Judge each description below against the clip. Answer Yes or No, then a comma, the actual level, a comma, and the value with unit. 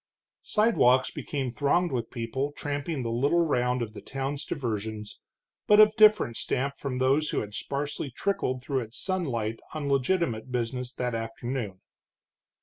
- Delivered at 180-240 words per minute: No, average, 145 wpm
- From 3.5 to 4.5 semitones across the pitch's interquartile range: Yes, average, 3.8 semitones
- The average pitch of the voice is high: No, low, 130 Hz